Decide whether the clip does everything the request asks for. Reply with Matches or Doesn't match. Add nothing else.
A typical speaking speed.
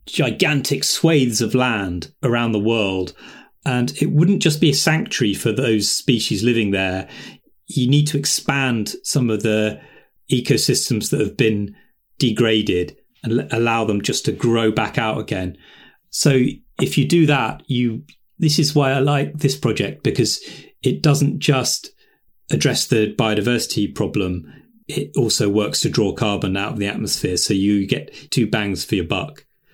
Matches